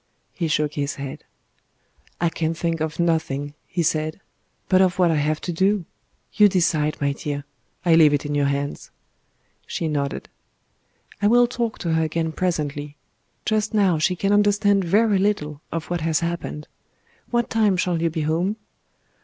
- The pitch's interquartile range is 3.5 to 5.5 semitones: Yes, average, 4.1 semitones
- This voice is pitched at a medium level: Yes, medium, 165 Hz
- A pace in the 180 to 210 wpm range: No, average, 170 wpm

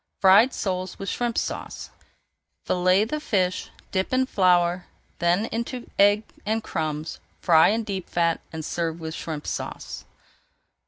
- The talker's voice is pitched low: No, medium, 185 Hz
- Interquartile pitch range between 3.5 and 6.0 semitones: Yes, average, 4.0 semitones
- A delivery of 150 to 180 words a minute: No, average, 140 wpm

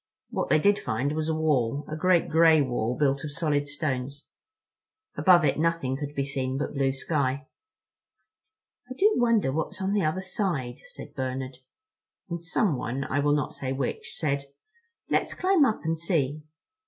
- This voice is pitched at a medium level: Yes, medium, 150 Hz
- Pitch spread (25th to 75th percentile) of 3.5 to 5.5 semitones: Yes, average, 4.2 semitones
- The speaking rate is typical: Yes, average, 160 wpm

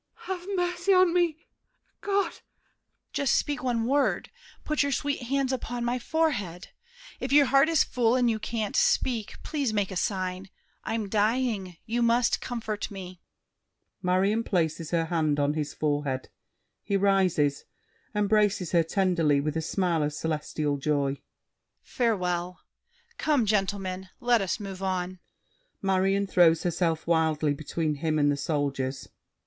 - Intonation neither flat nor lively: No, wide, 6.7 semitones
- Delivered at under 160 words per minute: Yes, average, 145 wpm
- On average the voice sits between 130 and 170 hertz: No, high, 195 Hz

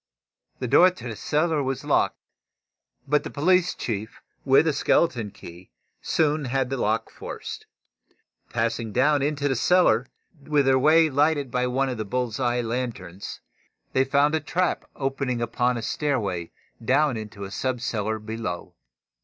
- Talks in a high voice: No, low, 130 Hz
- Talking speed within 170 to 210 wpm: No, average, 155 wpm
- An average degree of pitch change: Yes, average, 4.4 semitones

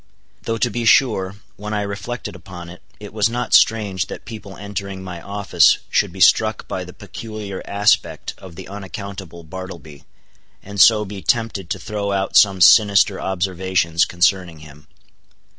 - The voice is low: Yes, low, 100 Hz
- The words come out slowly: No, average, 160 wpm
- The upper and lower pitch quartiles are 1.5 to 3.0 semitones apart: Yes, narrow, 2.4 semitones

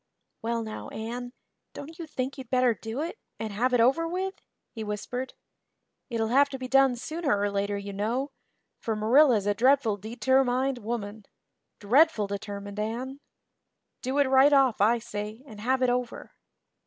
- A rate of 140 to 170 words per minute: Yes, average, 165 wpm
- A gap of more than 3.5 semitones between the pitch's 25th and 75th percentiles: Yes, average, 3.9 semitones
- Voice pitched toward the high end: Yes, high, 245 Hz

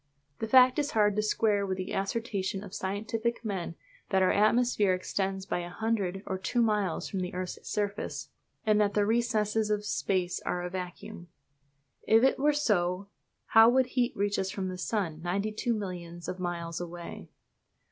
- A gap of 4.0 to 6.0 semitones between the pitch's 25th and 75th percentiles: No, average, 3.2 semitones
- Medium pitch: No, high, 200 Hz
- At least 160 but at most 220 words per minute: Yes, average, 180 wpm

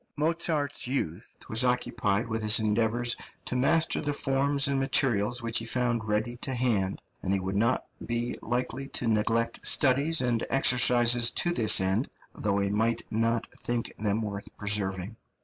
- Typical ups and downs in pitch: Yes, average, 3.1 semitones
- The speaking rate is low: No, average, 160 wpm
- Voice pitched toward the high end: No, low, 115 Hz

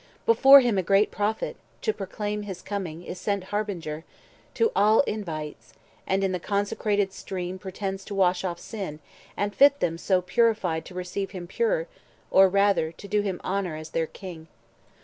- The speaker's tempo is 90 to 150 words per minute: No, average, 175 wpm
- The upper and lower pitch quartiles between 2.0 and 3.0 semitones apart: Yes, narrow, 2.6 semitones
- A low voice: No, high, 195 Hz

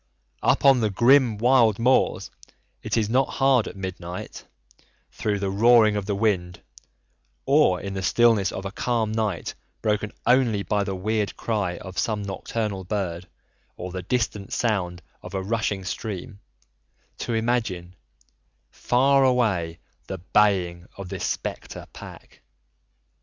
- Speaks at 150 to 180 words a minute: No, average, 140 wpm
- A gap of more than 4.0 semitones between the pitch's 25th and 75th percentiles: No, average, 3.7 semitones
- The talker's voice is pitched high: No, low, 105 Hz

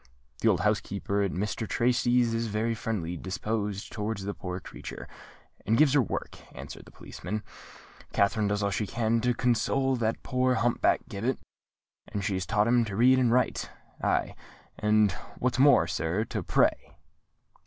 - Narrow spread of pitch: No, average, 3.2 semitones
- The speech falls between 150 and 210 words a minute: Yes, average, 165 wpm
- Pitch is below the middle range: Yes, low, 110 Hz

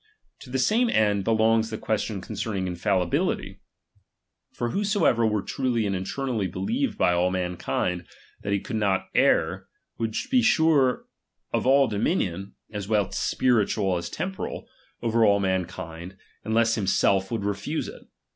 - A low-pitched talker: Yes, low, 105 Hz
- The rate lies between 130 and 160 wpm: Yes, average, 145 wpm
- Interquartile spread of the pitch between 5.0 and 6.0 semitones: No, average, 4.2 semitones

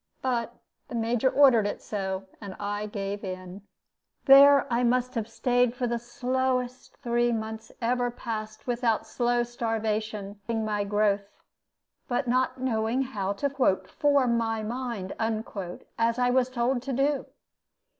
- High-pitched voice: Yes, high, 235 Hz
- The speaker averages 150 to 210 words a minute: No, average, 140 wpm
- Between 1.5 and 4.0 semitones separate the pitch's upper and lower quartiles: Yes, average, 2.7 semitones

